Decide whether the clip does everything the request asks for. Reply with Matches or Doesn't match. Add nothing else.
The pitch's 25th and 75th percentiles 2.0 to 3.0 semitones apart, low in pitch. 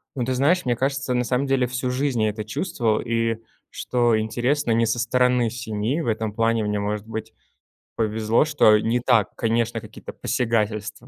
Matches